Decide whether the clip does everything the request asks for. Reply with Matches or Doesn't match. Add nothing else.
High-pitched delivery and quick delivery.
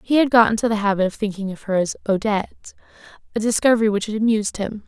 Matches